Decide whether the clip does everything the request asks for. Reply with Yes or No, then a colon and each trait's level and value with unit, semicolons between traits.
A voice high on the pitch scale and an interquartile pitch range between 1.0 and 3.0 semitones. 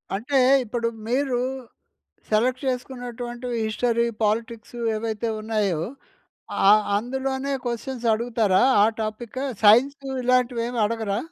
Yes: high, 235 Hz; narrow, 2.6 semitones